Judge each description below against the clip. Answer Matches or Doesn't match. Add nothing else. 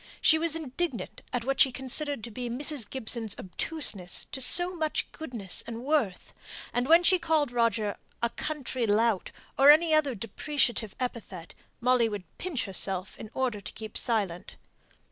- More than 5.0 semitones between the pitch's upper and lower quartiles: Matches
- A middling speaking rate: Matches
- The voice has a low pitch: Doesn't match